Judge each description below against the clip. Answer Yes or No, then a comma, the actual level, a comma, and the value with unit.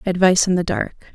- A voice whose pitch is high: No, medium, 180 Hz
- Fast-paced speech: Yes, fast, 210 wpm